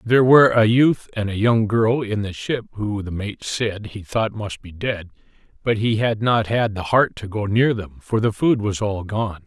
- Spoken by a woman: No, male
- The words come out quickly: Yes, fast, 235 wpm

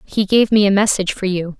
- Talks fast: Yes, fast, 265 wpm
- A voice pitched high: Yes, high, 200 Hz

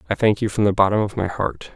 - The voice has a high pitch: No, low, 105 Hz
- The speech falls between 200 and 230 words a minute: No, fast, 305 wpm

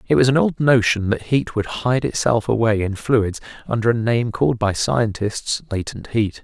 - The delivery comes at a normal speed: Yes, average, 195 wpm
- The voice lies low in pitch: Yes, low, 115 Hz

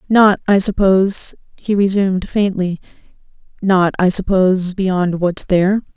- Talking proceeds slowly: Yes, slow, 110 wpm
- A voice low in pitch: No, high, 190 Hz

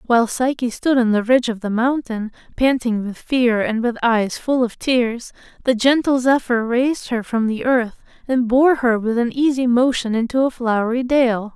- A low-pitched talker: No, high, 240 Hz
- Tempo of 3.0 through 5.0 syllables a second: Yes, 4.7 syllables/s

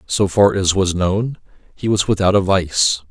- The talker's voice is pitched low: Yes, very low, 95 Hz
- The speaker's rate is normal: Yes, average, 195 wpm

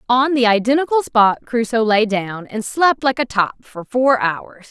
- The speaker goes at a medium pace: Yes, average, 190 wpm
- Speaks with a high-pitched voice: Yes, high, 235 Hz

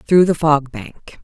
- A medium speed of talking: Yes, average, 195 wpm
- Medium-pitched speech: Yes, medium, 150 Hz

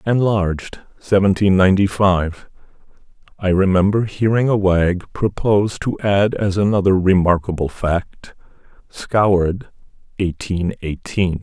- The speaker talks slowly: Yes, slow, 100 wpm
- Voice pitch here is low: Yes, very low, 95 Hz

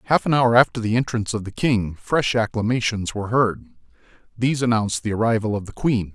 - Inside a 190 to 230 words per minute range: Yes, average, 195 wpm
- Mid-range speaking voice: No, low, 110 Hz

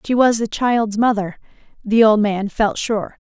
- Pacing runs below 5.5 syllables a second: Yes, 4.2 syllables/s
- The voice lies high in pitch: Yes, high, 220 Hz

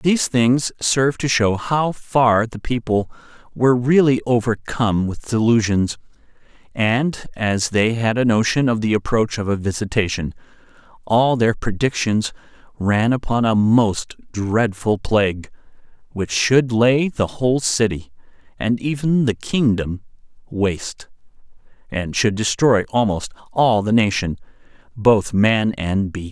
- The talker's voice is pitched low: Yes, low, 115 Hz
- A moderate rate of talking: No, slow, 130 wpm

